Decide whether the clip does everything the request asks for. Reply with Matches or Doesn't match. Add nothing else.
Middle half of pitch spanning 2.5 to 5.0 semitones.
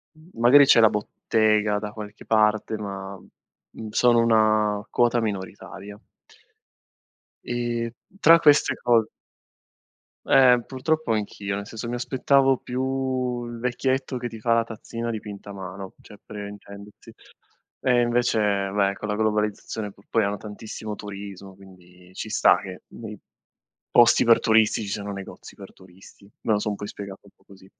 Matches